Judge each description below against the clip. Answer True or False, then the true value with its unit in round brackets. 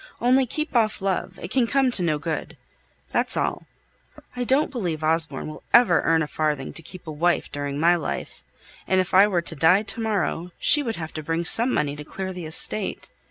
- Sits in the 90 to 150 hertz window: False (175 Hz)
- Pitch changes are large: True (5.8 semitones)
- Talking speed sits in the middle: False (210 wpm)